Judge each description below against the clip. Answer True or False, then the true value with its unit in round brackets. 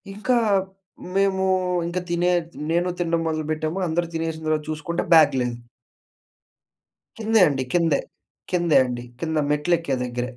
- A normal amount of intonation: False (2.2 semitones)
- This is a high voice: False (165 Hz)